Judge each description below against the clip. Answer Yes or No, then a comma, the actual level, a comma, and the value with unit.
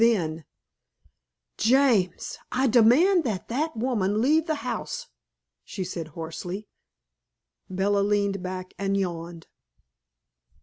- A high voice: Yes, high, 200 Hz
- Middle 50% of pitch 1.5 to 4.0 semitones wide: No, average, 5.3 semitones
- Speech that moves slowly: Yes, slow, 100 wpm